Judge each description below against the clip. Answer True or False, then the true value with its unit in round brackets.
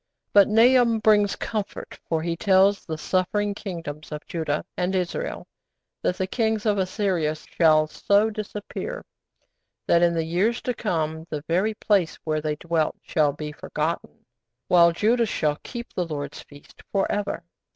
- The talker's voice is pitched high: False (180 Hz)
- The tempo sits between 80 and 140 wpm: False (155 wpm)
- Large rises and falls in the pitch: False (4.7 semitones)